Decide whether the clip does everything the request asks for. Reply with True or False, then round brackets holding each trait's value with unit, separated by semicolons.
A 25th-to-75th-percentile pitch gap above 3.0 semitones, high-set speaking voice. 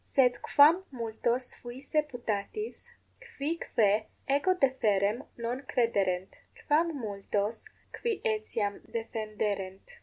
True (5.2 semitones; 235 Hz)